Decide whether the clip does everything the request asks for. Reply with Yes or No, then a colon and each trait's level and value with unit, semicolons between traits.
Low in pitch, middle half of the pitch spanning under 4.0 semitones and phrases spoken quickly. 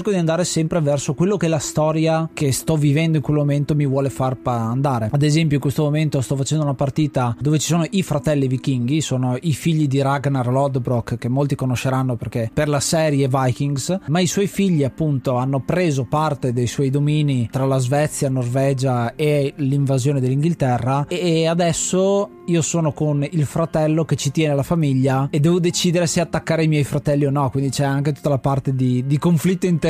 No: medium, 145 Hz; average, 2.9 semitones; fast, 195 wpm